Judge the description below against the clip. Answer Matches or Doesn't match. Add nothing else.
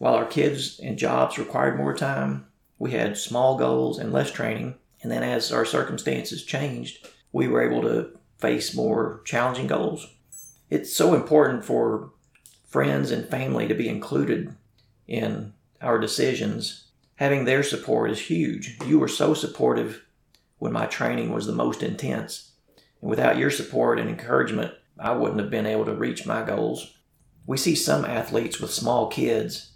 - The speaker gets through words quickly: Doesn't match